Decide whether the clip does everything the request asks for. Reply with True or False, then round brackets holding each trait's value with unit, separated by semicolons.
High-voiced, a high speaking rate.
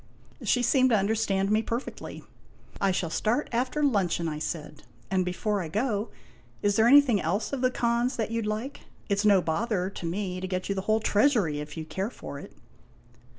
True (205 Hz; 220 wpm)